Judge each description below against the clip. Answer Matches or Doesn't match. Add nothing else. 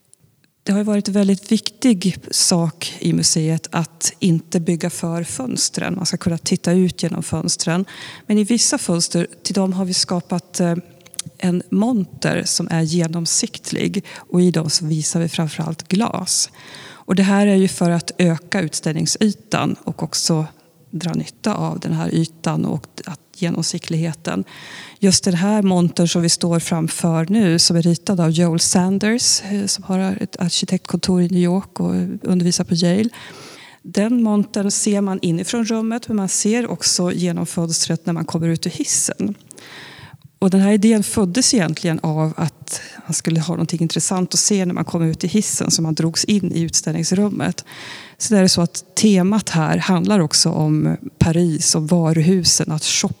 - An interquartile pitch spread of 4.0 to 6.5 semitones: Doesn't match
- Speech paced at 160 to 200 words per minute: Matches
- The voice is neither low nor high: Matches